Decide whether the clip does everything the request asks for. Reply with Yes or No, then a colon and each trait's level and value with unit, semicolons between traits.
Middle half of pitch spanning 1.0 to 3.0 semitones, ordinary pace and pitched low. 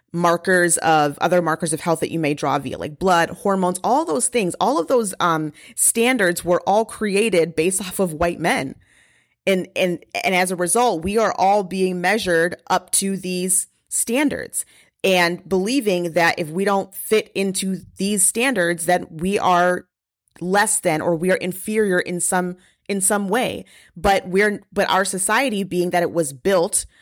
No: narrow, 2.6 semitones; average, 175 wpm; medium, 185 Hz